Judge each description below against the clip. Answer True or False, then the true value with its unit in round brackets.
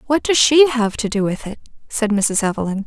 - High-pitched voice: True (230 Hz)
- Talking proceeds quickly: True (230 wpm)